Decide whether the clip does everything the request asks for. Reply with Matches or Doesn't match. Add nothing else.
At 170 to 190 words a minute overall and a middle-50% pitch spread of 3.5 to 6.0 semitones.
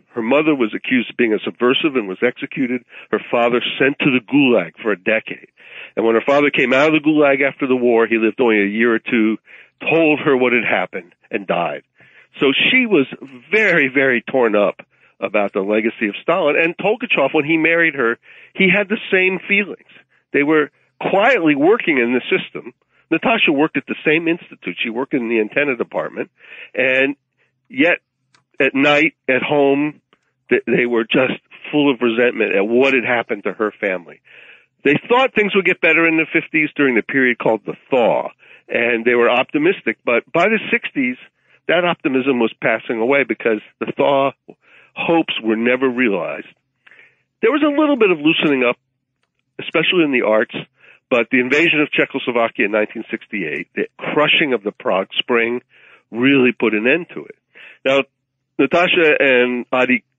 Matches